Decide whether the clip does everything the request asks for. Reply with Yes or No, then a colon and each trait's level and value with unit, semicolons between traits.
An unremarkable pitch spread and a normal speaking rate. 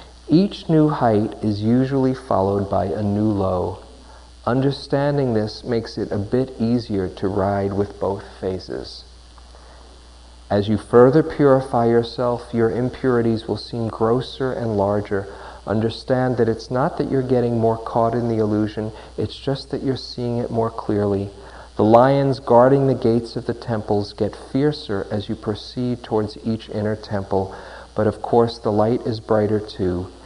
Yes: average, 3.5 semitones; average, 155 wpm